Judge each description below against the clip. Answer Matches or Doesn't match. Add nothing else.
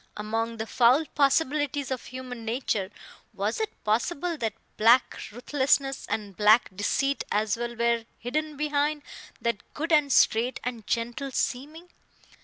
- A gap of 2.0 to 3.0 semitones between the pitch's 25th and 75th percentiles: Doesn't match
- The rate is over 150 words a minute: Doesn't match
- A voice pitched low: Doesn't match